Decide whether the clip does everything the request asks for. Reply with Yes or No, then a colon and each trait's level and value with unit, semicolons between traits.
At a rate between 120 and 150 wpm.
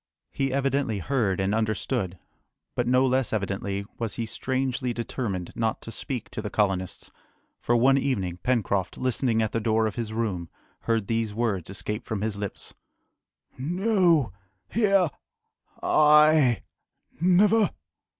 Yes: slow, 135 wpm